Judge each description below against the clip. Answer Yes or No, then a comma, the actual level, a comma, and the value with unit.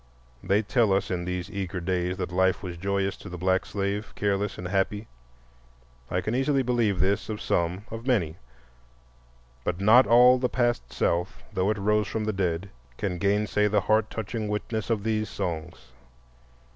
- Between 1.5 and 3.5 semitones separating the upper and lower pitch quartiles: Yes, average, 2.8 semitones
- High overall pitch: No, low, 100 Hz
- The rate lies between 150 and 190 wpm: Yes, average, 170 wpm